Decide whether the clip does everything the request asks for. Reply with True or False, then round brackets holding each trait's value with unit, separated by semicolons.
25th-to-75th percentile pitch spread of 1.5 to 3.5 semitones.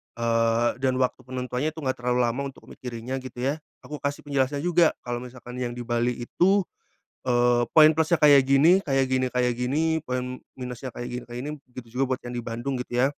True (2.4 semitones)